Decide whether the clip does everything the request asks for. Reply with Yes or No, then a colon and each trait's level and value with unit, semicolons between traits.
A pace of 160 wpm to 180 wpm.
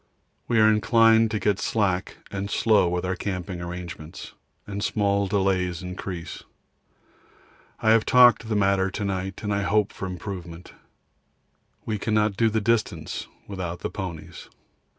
No: average, 140 wpm